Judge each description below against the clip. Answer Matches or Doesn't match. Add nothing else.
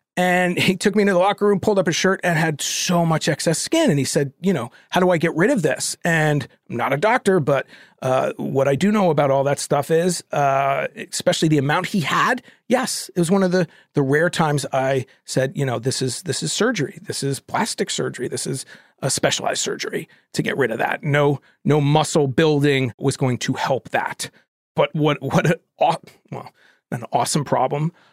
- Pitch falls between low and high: Matches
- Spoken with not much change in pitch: Doesn't match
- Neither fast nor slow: Doesn't match